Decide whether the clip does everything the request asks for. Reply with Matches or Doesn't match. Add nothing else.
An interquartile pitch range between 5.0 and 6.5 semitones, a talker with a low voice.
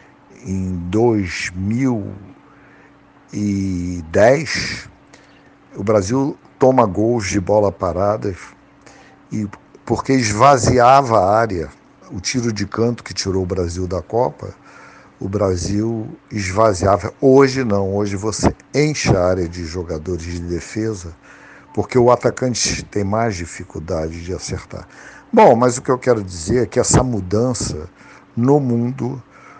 Doesn't match